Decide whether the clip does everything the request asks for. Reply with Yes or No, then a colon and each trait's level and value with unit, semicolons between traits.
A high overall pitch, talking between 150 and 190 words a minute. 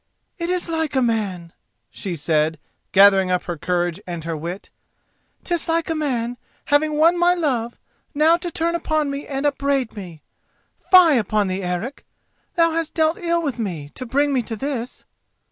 Yes: very high, 265 Hz; average, 175 wpm